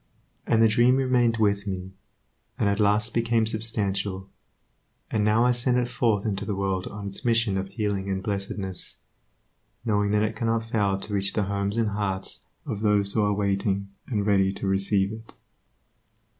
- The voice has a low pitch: Yes, low, 105 Hz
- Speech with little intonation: Yes, narrow, 2.3 semitones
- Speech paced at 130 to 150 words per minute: No, average, 175 wpm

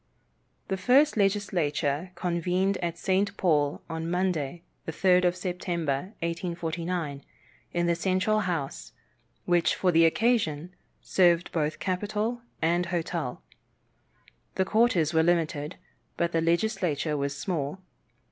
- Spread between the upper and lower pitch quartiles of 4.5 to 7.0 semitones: No, narrow, 2.5 semitones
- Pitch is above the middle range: No, medium, 175 Hz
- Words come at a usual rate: No, slow, 120 wpm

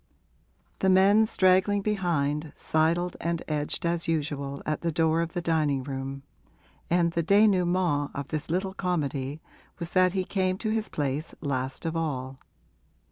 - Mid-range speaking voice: Yes, medium, 165 Hz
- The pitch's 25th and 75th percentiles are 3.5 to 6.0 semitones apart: Yes, average, 4.1 semitones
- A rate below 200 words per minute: Yes, average, 150 wpm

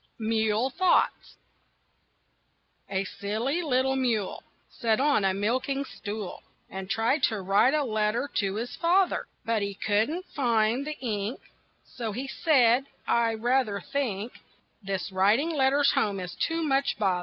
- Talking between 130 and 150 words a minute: Yes, average, 140 wpm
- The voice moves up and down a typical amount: Yes, average, 4.8 semitones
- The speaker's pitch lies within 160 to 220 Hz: No, high, 230 Hz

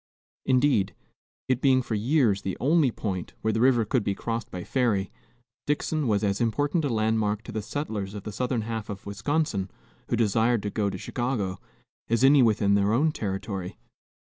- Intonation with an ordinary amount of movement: Yes, average, 4.2 semitones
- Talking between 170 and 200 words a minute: Yes, average, 180 wpm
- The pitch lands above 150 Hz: No, low, 110 Hz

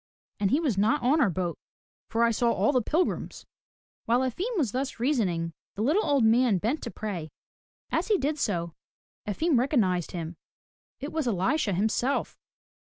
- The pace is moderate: Yes, average, 165 wpm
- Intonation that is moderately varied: No, wide, 6.5 semitones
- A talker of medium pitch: No, high, 235 Hz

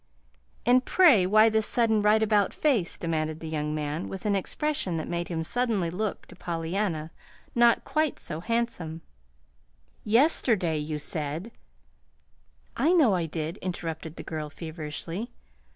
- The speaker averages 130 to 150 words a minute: Yes, average, 145 wpm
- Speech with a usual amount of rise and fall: No, wide, 5.9 semitones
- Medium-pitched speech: Yes, medium, 180 Hz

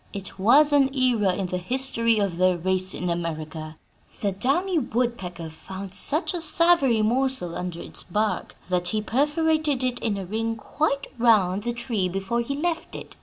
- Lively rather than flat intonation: Yes, wide, 6.4 semitones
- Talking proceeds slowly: No, average, 170 wpm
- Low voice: No, high, 220 Hz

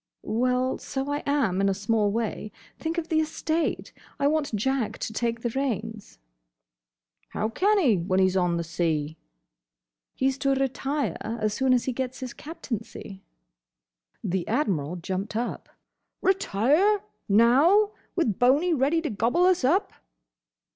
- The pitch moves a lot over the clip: Yes, wide, 6.2 semitones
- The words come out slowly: No, average, 145 wpm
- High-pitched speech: Yes, very high, 250 Hz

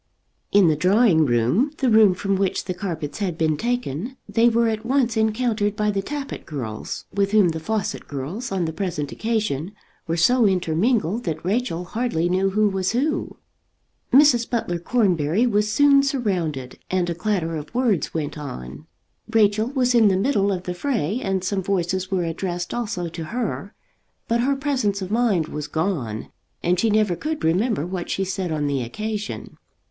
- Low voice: No, high, 195 Hz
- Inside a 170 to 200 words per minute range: Yes, average, 175 wpm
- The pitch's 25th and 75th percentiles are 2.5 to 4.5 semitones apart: No, wide, 5.4 semitones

